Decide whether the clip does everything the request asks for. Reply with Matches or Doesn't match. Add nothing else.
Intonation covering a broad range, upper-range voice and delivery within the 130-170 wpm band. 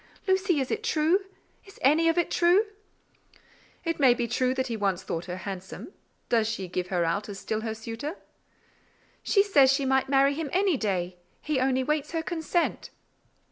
Doesn't match